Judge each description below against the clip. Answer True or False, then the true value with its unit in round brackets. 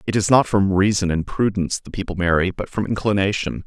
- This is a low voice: True (100 Hz)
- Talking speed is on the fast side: True (215 wpm)